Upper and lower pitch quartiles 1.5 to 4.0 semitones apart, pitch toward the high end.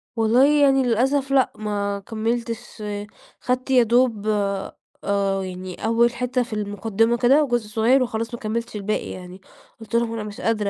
Yes: average, 2.9 semitones; high, 230 Hz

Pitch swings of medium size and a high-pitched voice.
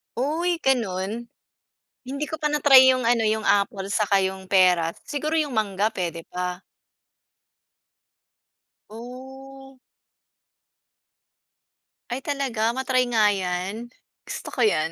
No: wide, 5.7 semitones; high, 225 Hz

